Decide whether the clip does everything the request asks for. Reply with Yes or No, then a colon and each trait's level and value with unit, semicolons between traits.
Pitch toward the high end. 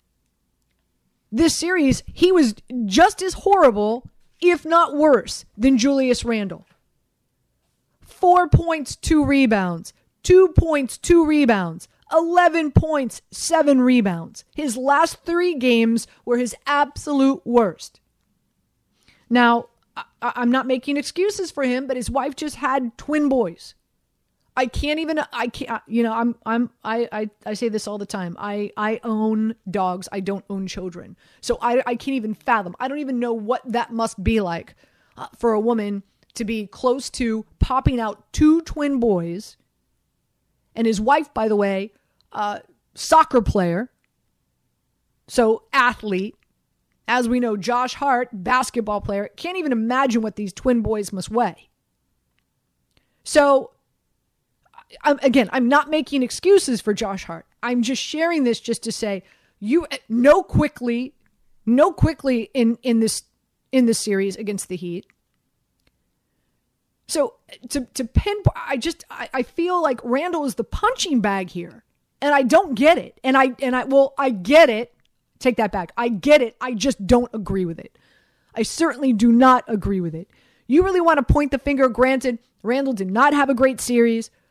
Yes: high, 245 Hz